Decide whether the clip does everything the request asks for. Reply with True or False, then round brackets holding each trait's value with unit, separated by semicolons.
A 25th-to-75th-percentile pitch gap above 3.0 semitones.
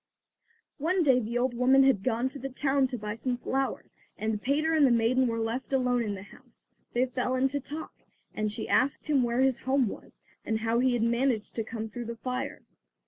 False (2.7 semitones)